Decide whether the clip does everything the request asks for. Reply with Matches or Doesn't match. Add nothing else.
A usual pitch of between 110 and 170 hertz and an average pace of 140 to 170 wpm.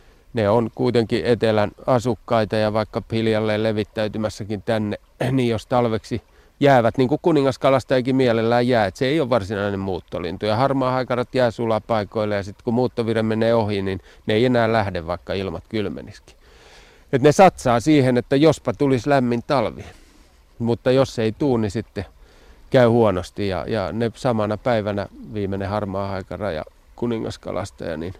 Matches